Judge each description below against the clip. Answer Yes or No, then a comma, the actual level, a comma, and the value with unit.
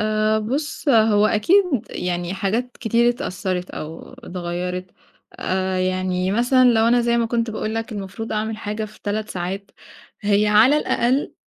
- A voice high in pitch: Yes, high, 215 Hz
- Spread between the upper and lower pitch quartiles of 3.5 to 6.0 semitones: Yes, average, 3.8 semitones